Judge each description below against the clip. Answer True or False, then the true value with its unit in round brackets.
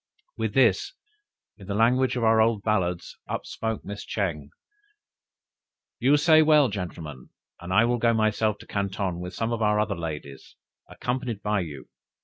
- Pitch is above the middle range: False (105 Hz)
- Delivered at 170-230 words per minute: False (155 wpm)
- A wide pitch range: False (4.4 semitones)